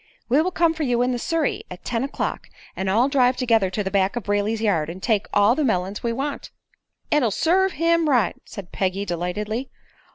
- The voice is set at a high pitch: Yes, high, 230 Hz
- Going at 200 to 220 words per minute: Yes, fast, 205 wpm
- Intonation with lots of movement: Yes, wide, 5.8 semitones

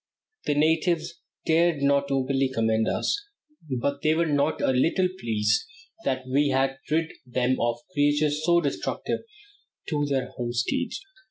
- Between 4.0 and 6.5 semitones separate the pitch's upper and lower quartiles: No, average, 3.3 semitones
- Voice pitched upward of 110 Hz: Yes, medium, 140 Hz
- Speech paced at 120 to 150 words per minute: Yes, average, 140 wpm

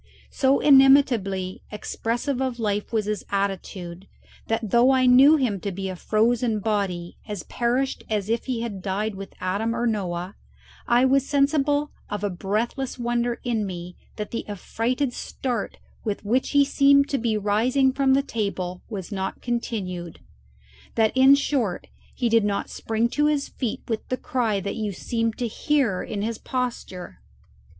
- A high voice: Yes, high, 225 Hz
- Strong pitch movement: No, average, 4.3 semitones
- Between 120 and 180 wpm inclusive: Yes, average, 165 wpm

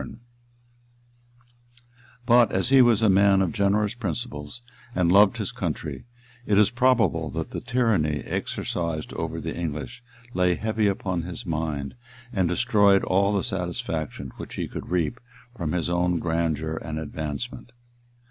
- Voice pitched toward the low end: Yes, very low, 90 Hz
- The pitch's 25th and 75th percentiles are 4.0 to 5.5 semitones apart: Yes, average, 4.7 semitones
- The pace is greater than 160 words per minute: No, average, 145 wpm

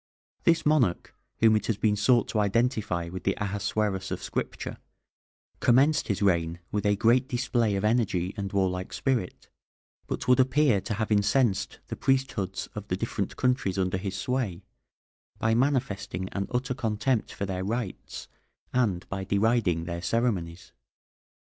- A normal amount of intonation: Yes, average, 4.4 semitones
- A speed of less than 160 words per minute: Yes, average, 150 wpm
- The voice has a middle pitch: No, low, 105 Hz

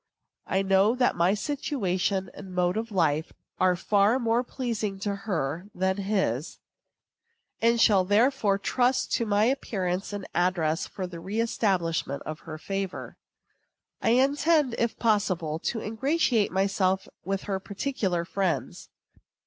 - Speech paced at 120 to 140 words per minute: Yes, slow, 135 wpm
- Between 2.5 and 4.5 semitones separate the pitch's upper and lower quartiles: Yes, average, 3.9 semitones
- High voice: Yes, high, 195 Hz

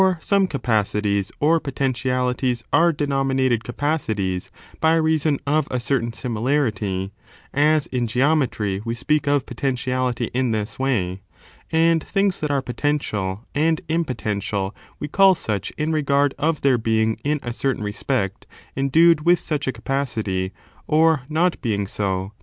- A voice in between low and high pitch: No, low, 130 Hz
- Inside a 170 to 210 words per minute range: No, average, 140 wpm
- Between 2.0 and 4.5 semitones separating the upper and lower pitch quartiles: No, wide, 5.5 semitones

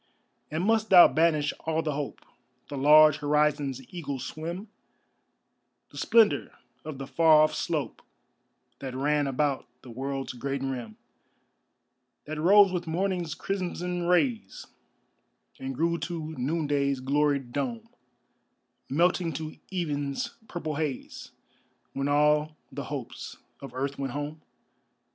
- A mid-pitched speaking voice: Yes, medium, 150 Hz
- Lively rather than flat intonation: No, average, 3.4 semitones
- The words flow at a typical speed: No, slow, 120 wpm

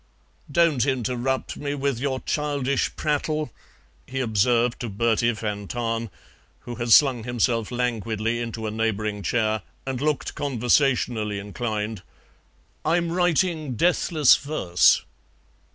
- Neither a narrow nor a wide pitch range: Yes, average, 4.2 semitones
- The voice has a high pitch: No, low, 120 Hz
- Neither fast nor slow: No, slow, 115 wpm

